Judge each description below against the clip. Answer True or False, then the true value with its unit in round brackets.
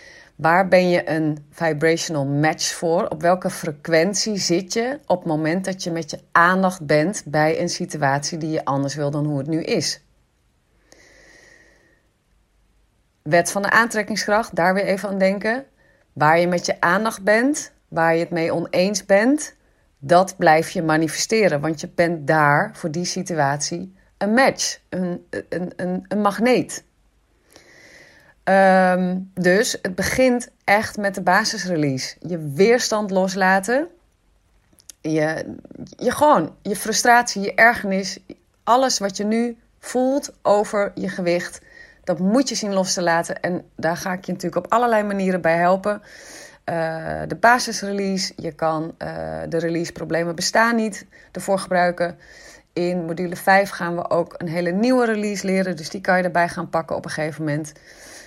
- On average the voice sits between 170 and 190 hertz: True (185 Hz)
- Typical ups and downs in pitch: True (3.9 semitones)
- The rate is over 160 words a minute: False (155 wpm)